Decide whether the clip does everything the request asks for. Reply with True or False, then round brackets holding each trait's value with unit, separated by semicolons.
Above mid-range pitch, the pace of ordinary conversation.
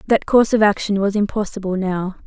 True (200 Hz; 185 wpm)